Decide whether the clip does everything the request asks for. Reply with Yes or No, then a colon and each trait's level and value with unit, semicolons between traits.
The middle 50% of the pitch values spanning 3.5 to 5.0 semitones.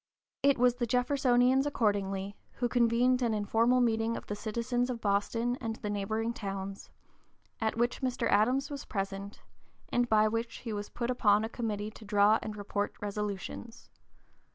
No: average, 2.9 semitones